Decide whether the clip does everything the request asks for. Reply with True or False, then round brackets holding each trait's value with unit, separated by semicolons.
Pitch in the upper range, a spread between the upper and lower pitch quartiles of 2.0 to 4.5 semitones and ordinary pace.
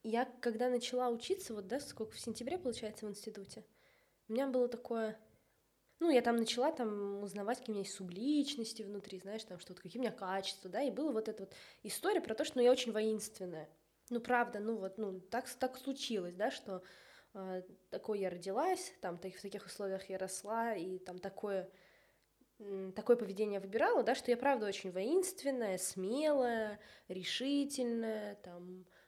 False (220 Hz; 4.2 semitones; 175 wpm)